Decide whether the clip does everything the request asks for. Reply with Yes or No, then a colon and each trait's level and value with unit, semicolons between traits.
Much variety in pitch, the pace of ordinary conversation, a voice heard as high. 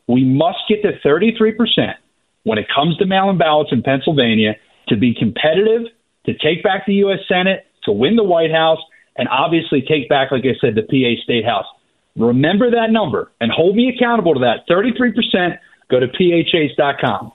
No: wide, 8.3 semitones; average, 175 wpm; medium, 170 Hz